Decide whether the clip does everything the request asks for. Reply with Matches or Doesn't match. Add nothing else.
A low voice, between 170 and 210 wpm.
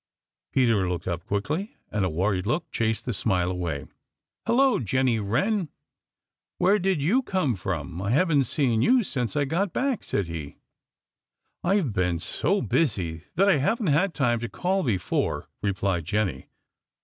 Doesn't match